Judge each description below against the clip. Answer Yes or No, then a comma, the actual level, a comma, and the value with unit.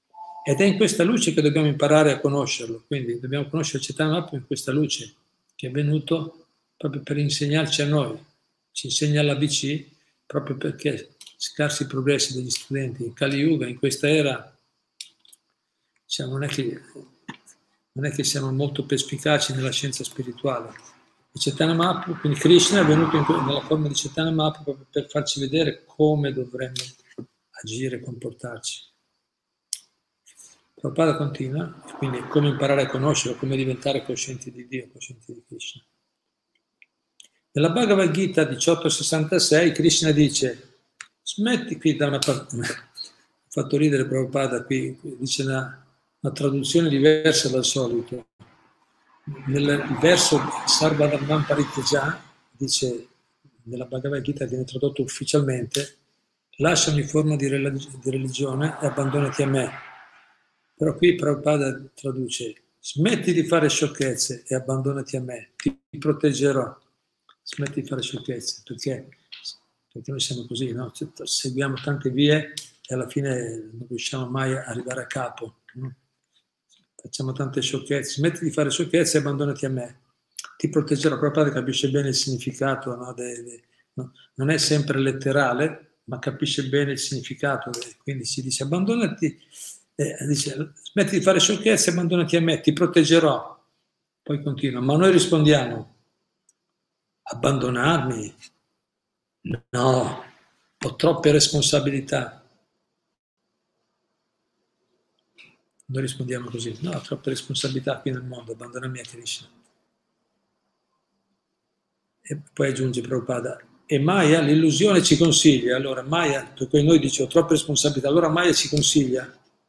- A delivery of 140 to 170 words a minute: No, average, 130 wpm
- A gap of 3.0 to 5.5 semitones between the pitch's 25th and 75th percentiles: No, narrow, 2.6 semitones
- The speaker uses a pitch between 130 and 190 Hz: Yes, medium, 140 Hz